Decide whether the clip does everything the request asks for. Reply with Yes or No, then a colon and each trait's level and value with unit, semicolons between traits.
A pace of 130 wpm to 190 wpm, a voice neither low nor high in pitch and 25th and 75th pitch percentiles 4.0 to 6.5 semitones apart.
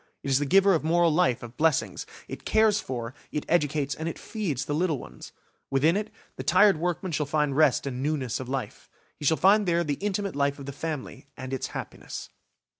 No: fast, 205 wpm; medium, 155 Hz; average, 4.5 semitones